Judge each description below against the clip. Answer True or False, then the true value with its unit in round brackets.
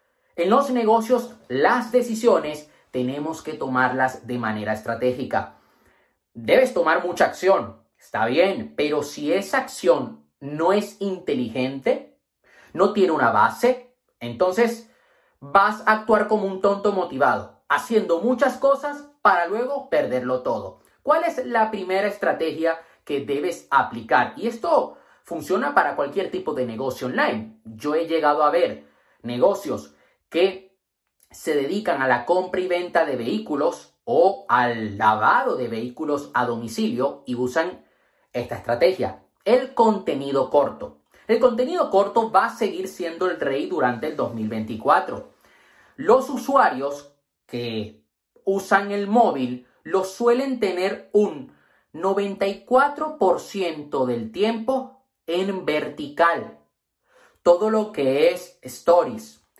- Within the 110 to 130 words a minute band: True (125 wpm)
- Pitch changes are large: True (8.4 semitones)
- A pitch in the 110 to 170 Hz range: False (190 Hz)